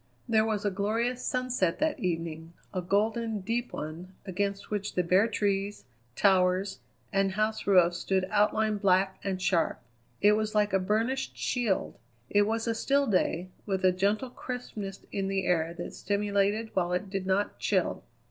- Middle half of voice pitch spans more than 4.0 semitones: No, average, 2.7 semitones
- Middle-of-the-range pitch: No, high, 200 Hz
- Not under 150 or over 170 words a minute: Yes, average, 165 wpm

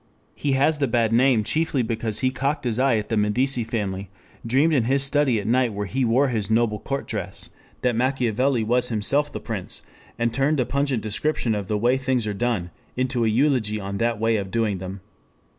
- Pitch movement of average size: Yes, average, 3.8 semitones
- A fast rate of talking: Yes, fast, 210 wpm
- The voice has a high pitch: No, low, 120 Hz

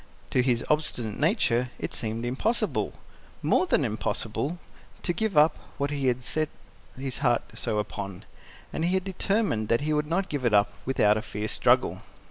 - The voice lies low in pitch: Yes, low, 130 Hz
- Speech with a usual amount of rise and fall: No, wide, 5.8 semitones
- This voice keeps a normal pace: Yes, average, 175 wpm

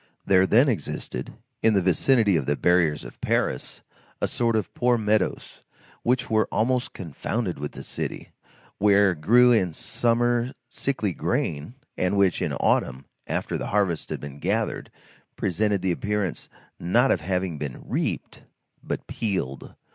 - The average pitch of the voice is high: No, low, 100 Hz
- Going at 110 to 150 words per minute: Yes, average, 145 wpm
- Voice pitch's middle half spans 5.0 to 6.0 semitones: Yes, average, 5.3 semitones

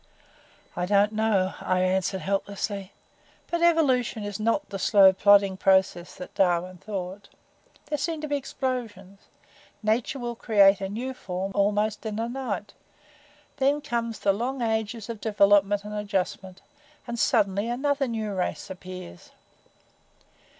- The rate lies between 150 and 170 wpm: No, slow, 135 wpm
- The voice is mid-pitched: No, high, 205 Hz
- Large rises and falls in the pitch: No, average, 3.5 semitones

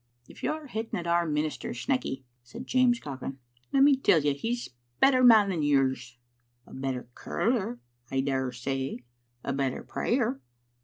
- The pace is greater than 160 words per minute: Yes, average, 170 wpm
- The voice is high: No, medium, 140 Hz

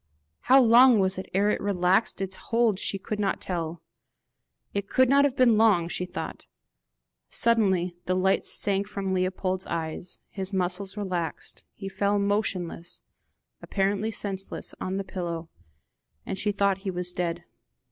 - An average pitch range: No, narrow, 2.3 semitones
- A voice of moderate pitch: No, high, 195 Hz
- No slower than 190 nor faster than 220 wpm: No, average, 155 wpm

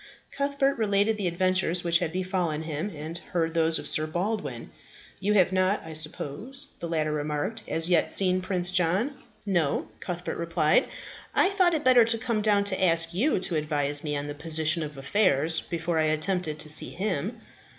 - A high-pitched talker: No, medium, 175 Hz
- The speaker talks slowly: No, average, 180 wpm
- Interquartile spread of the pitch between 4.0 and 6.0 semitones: Yes, average, 4.4 semitones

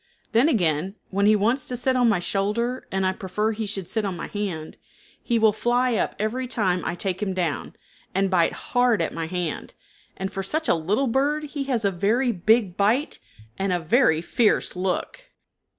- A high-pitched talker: Yes, high, 205 Hz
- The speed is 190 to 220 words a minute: Yes, average, 200 wpm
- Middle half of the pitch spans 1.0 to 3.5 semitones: No, average, 4.6 semitones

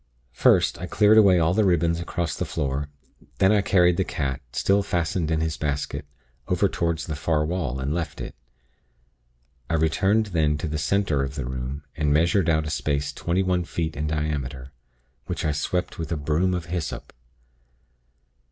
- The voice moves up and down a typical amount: Yes, average, 3.3 semitones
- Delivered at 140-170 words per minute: No, average, 180 wpm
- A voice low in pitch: Yes, very low, 80 Hz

